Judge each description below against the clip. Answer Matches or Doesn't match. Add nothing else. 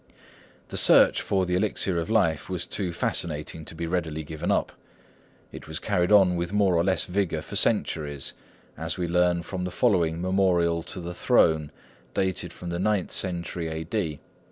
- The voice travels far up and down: Doesn't match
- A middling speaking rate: Matches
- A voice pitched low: Matches